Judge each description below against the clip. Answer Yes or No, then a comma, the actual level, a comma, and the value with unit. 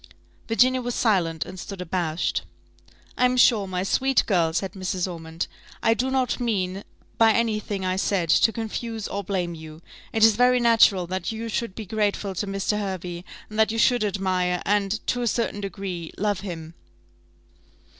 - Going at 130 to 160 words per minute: No, average, 175 wpm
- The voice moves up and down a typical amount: Yes, average, 3.7 semitones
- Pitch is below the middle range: No, high, 200 Hz